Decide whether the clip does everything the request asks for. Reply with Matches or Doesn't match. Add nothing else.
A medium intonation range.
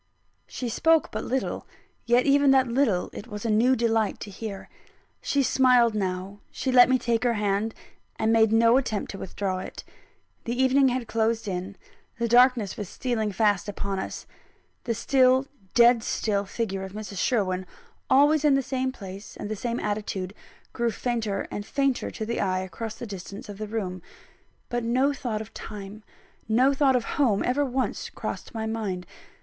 Matches